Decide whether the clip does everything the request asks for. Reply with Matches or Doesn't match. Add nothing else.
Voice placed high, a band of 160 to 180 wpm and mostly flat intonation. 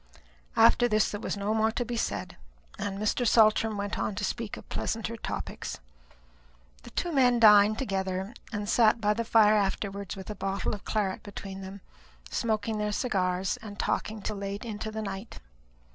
Matches